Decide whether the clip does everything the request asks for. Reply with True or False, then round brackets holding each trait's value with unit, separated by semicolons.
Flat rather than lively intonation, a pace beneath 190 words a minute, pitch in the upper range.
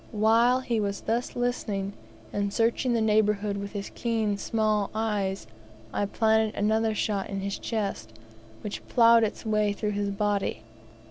True (1.9 semitones; 150 wpm; 210 Hz)